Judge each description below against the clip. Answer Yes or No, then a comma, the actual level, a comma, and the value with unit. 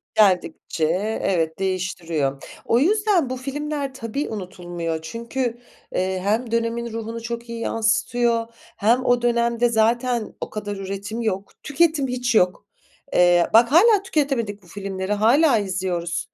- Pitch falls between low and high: No, high, 230 Hz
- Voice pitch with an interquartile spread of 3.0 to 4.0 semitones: No, average, 4.5 semitones